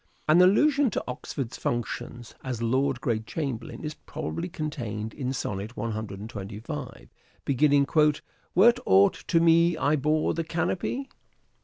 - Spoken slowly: Yes, slow, 130 wpm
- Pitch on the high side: No, low, 135 Hz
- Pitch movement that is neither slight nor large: No, wide, 6.6 semitones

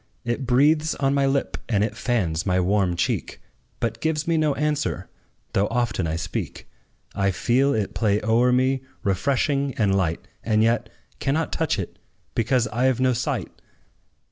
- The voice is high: No, low, 120 Hz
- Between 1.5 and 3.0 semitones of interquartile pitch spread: No, average, 5.1 semitones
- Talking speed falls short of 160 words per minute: No, average, 165 wpm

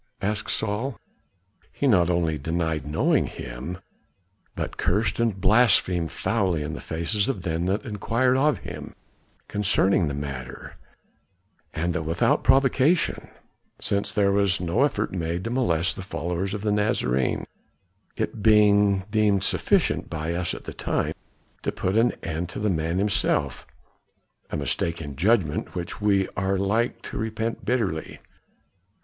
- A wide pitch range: No, average, 4.4 semitones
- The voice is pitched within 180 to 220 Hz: No, very low, 95 Hz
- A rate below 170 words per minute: Yes, average, 145 wpm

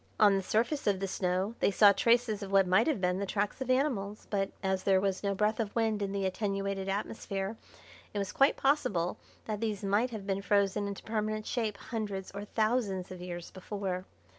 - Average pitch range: No, narrow, 2.0 semitones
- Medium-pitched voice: No, high, 200 Hz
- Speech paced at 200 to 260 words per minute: Yes, fast, 205 wpm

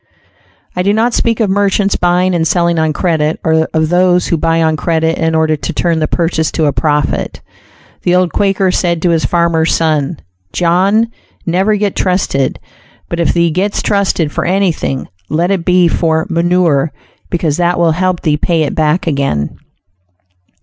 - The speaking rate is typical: Yes, average, 175 wpm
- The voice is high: No, medium, 170 Hz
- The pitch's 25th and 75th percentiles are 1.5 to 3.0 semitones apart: Yes, narrow, 2.4 semitones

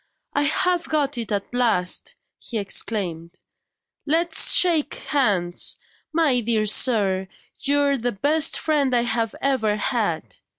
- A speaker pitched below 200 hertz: No, high, 240 Hz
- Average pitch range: No, wide, 5.9 semitones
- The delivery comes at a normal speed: No, slow, 125 wpm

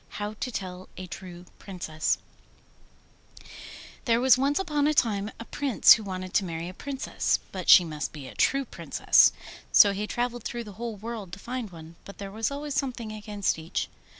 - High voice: Yes, high, 210 Hz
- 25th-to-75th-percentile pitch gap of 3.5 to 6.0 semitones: Yes, average, 4.8 semitones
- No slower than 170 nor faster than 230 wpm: Yes, average, 185 wpm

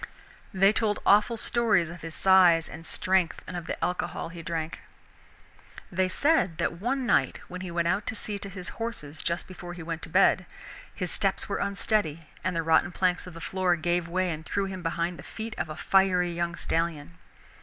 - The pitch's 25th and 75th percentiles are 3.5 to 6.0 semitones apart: No, average, 2.7 semitones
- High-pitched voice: No, medium, 180 Hz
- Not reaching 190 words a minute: No, average, 200 wpm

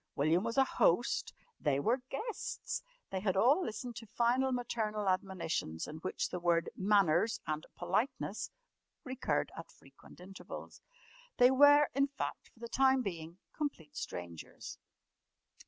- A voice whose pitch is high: Yes, high, 215 Hz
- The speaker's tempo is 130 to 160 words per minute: Yes, average, 140 wpm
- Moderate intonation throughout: No, wide, 7.1 semitones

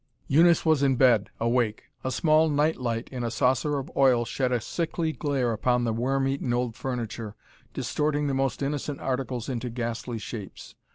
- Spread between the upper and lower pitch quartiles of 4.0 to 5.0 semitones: No, average, 3.2 semitones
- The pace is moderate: Yes, average, 170 wpm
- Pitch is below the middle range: Yes, low, 130 Hz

